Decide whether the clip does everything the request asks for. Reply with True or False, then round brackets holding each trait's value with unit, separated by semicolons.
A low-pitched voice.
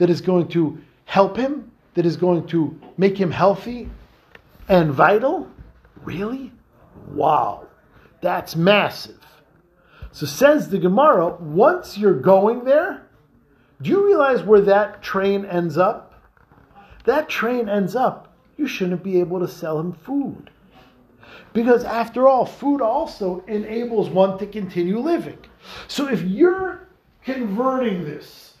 False (200 Hz)